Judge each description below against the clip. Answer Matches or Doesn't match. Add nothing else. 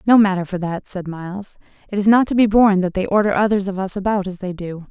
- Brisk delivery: Matches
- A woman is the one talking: Matches